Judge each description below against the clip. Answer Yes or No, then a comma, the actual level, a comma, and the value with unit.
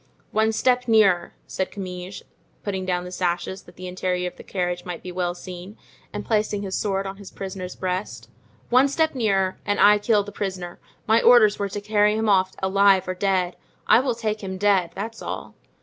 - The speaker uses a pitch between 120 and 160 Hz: No, high, 195 Hz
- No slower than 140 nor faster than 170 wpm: No, average, 195 wpm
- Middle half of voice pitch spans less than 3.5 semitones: Yes, narrow, 2.5 semitones